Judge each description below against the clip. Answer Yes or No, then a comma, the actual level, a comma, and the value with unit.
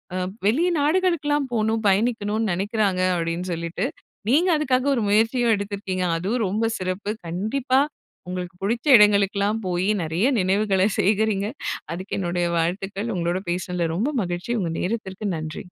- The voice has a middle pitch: No, high, 200 Hz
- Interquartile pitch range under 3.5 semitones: No, average, 3.8 semitones